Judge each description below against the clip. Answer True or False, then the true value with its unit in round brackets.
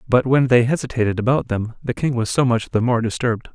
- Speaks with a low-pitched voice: True (120 Hz)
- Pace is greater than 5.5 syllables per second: True (6.1 syllables/s)